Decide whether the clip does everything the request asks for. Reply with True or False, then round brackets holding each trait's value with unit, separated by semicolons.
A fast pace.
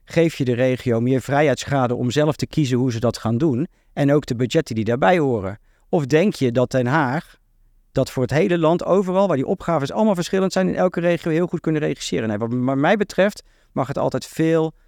True (220 wpm)